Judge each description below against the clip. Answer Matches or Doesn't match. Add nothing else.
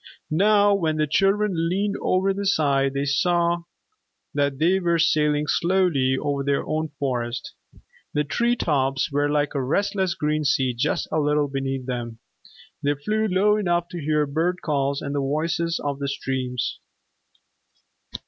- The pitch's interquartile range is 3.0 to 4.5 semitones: Matches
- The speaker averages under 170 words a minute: Matches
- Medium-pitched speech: Matches